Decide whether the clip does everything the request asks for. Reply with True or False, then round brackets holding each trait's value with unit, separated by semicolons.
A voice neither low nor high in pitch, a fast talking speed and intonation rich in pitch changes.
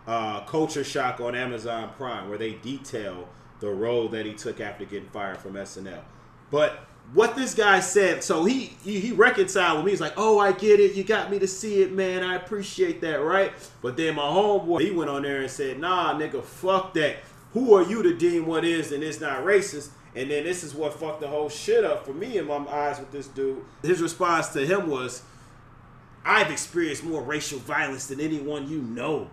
True (150 Hz; 215 wpm; 6.6 semitones)